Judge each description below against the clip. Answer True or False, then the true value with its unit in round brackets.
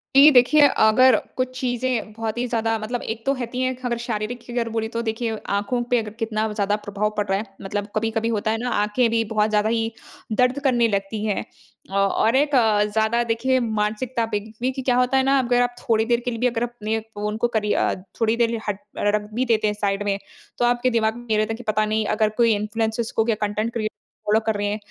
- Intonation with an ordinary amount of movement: False (2.3 semitones)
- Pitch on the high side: True (225 Hz)